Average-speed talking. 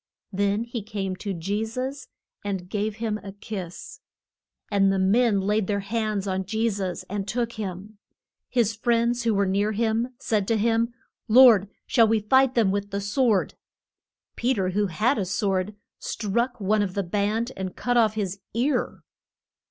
Yes: average, 170 wpm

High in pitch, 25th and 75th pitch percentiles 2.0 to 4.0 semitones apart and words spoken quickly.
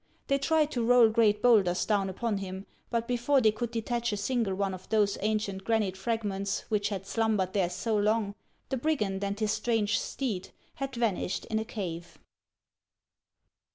No: high, 215 Hz; average, 3.1 semitones; average, 170 wpm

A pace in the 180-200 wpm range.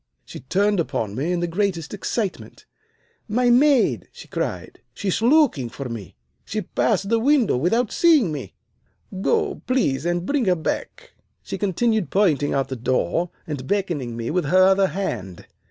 No: average, 170 wpm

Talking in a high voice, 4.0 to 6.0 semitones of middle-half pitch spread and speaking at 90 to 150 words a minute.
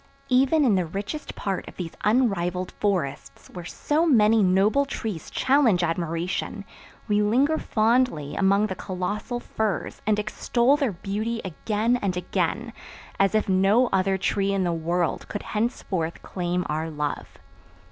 Yes: high, 200 Hz; average, 4.3 semitones; average, 145 wpm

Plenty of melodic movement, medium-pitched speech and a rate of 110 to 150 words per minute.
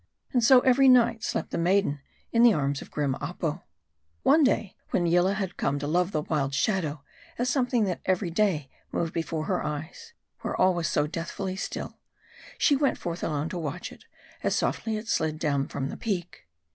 No: wide, 6.4 semitones; medium, 175 Hz; average, 195 wpm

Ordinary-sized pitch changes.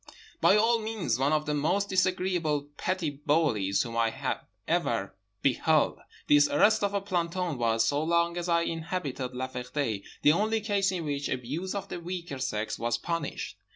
No: wide, 5.8 semitones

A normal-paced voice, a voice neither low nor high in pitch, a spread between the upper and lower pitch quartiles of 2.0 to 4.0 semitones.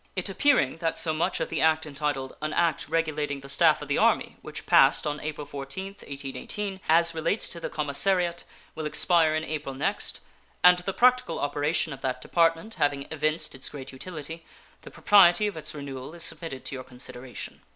Yes: average, 185 wpm; medium, 155 Hz; average, 3.3 semitones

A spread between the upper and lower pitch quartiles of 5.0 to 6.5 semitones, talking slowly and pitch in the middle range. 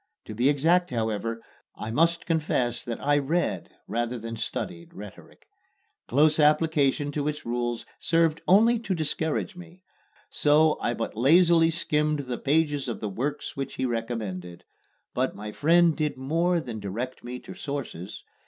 No: wide, 5.5 semitones; average, 155 wpm; medium, 145 Hz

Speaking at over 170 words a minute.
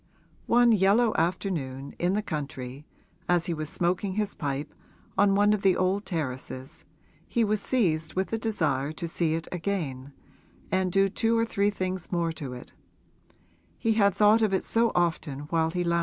Yes: average, 180 wpm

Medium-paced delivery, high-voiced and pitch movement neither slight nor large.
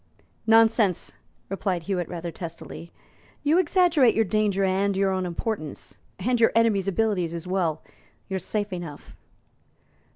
No: slow, 130 wpm; high, 195 Hz; average, 4.0 semitones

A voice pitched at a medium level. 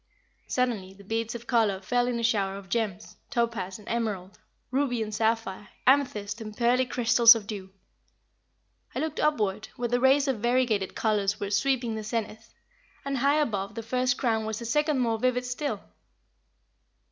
No: high, 230 Hz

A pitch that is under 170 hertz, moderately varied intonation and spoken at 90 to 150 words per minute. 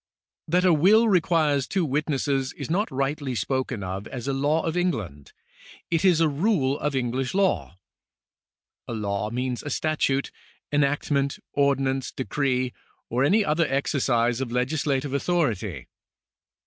Yes: medium, 140 Hz; average, 3.7 semitones; average, 140 wpm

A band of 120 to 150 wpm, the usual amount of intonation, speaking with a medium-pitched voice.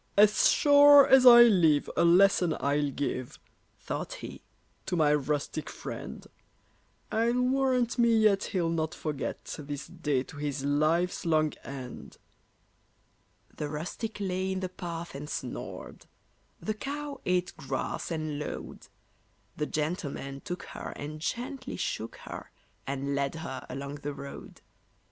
No: slow, 135 wpm; wide, 6.5 semitones; medium, 165 Hz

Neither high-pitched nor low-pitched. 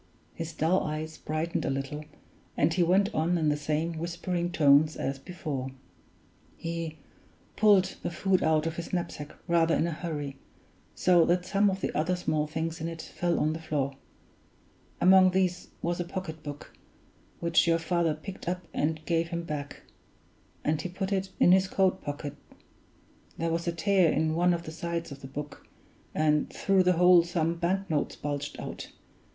Yes: medium, 165 Hz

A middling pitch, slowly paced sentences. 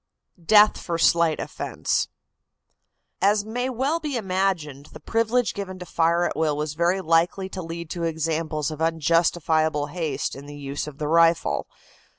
No: medium, 165 Hz; average, 160 wpm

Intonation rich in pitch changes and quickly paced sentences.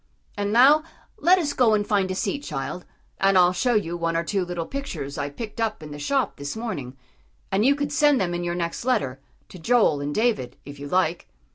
Yes: wide, 7.1 semitones; fast, 225 wpm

